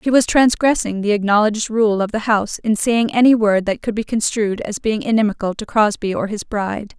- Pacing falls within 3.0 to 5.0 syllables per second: No, 5.5 syllables/s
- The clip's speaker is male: No, female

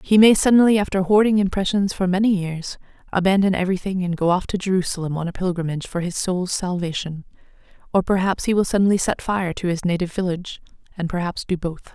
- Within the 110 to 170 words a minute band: No, average, 190 wpm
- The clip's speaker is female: Yes, female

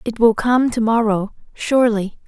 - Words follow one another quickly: No, average, 160 wpm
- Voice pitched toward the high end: Yes, high, 225 Hz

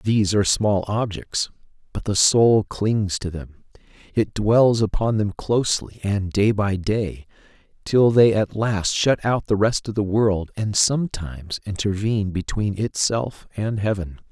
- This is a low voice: Yes, low, 105 Hz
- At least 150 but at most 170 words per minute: Yes, average, 155 wpm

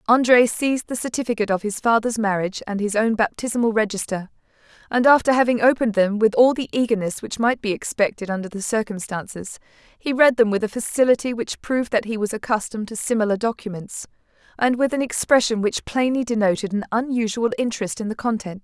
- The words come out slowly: No, average, 185 wpm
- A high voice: Yes, high, 225 Hz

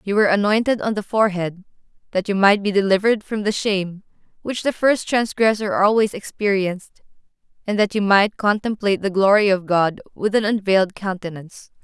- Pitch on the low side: No, high, 200 Hz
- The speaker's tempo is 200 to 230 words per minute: No, average, 165 wpm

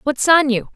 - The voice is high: Yes, very high, 275 Hz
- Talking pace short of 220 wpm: No, fast, 240 wpm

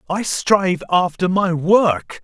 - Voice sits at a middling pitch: Yes, medium, 180 Hz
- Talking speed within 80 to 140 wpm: Yes, slow, 135 wpm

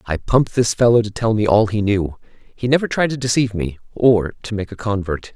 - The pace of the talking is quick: Yes, fast, 235 wpm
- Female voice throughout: No, male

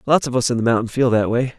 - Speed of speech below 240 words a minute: No, fast, 340 wpm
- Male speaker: Yes, male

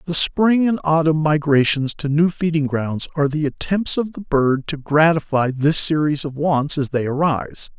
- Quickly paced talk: No, average, 185 wpm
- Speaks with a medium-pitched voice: Yes, medium, 150 Hz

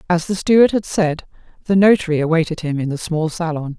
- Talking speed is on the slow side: No, fast, 205 wpm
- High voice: No, medium, 170 Hz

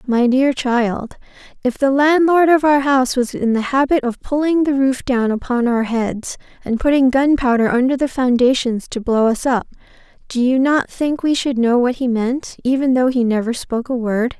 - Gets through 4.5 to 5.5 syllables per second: Yes, 4.8 syllables/s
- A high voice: Yes, very high, 255 Hz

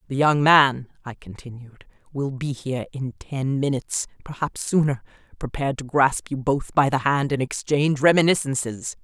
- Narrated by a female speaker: Yes, female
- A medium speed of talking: Yes, average, 145 wpm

